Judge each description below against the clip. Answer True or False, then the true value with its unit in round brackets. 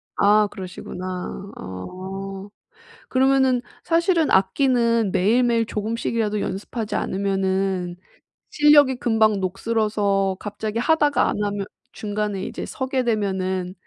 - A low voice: False (210 Hz)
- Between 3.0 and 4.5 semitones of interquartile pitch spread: True (3.8 semitones)